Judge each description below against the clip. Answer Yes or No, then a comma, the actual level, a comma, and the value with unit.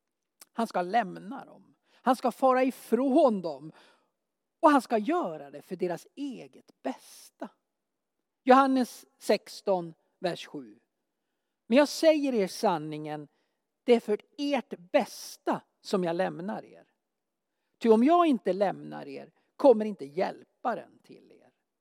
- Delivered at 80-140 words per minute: Yes, average, 130 wpm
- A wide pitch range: Yes, wide, 6.6 semitones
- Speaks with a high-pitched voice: Yes, high, 225 Hz